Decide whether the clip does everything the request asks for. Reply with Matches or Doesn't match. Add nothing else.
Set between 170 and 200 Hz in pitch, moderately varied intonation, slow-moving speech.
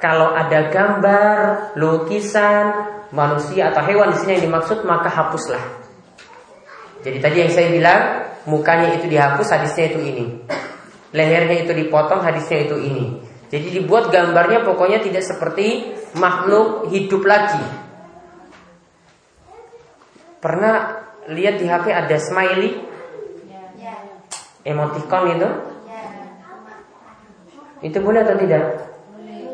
Doesn't match